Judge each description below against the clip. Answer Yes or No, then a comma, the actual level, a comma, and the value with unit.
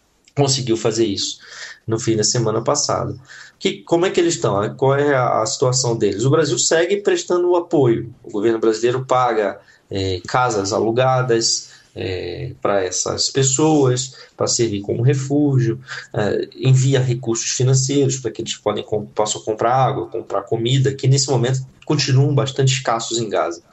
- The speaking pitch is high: No, low, 130 Hz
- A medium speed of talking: Yes, average, 150 wpm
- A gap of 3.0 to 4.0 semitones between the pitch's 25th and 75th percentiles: Yes, average, 3.3 semitones